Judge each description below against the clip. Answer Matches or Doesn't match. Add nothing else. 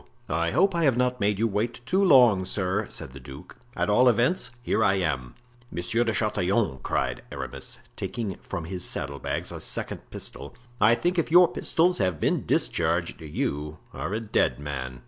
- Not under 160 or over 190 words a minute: Matches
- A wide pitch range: Matches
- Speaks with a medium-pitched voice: Doesn't match